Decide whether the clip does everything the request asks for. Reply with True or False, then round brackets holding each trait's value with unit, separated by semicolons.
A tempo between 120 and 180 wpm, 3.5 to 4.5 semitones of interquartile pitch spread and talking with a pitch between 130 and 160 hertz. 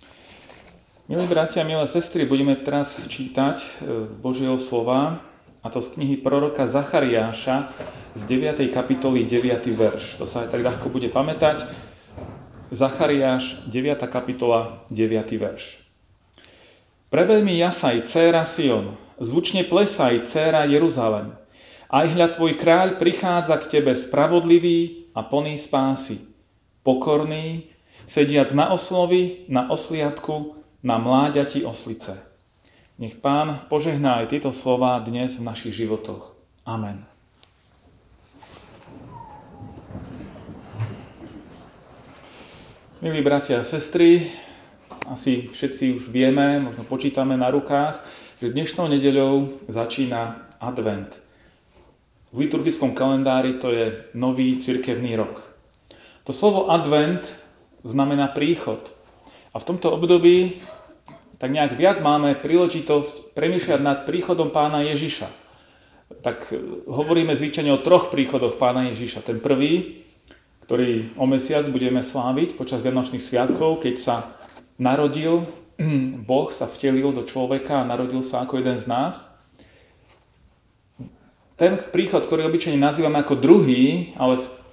False (110 wpm; 4.0 semitones; 135 Hz)